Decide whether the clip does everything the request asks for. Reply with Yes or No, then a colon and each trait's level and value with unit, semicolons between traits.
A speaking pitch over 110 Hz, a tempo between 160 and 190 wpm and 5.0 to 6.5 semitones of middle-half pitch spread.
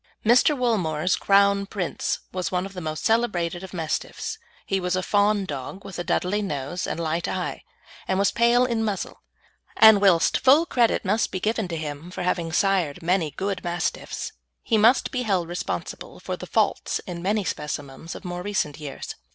No: medium, 185 Hz; average, 185 wpm; average, 3.6 semitones